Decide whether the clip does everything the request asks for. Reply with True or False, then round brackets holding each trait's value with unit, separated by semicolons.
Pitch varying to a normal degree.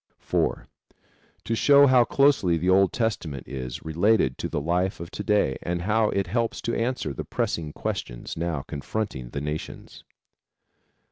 False (7.0 semitones)